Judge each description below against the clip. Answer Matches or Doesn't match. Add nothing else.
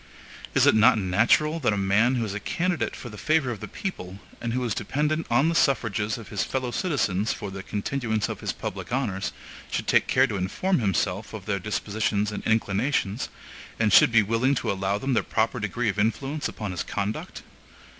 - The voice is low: Matches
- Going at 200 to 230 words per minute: Matches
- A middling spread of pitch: Matches